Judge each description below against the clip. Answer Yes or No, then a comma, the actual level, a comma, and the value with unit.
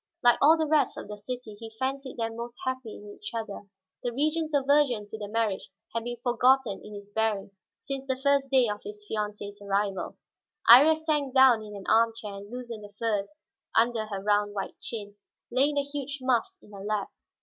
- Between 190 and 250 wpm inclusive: Yes, average, 200 wpm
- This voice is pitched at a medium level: No, high, 230 Hz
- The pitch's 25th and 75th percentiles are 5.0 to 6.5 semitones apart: No, average, 4.2 semitones